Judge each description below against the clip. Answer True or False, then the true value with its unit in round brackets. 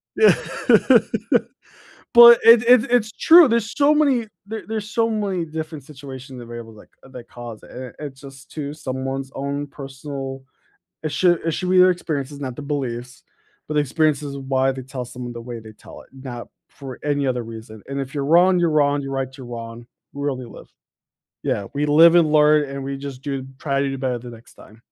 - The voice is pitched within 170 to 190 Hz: False (140 Hz)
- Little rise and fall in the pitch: False (3.6 semitones)